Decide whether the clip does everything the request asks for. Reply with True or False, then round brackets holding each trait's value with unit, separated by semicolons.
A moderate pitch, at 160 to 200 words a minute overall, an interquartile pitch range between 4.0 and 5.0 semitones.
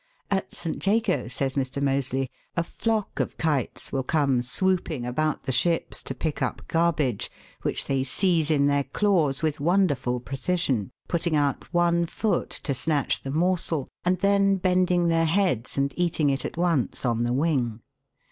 True (155 Hz; 165 wpm; 4.6 semitones)